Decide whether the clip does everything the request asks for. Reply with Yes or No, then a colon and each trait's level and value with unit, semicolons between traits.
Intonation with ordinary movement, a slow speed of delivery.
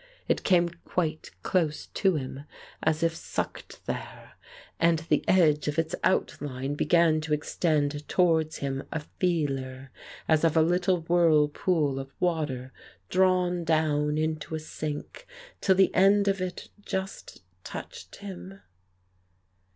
Yes: average, 3.1 semitones; slow, 130 wpm